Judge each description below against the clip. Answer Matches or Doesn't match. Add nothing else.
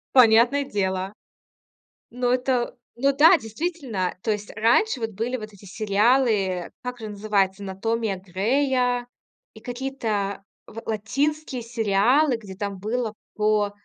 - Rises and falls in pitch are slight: Doesn't match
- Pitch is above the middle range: Matches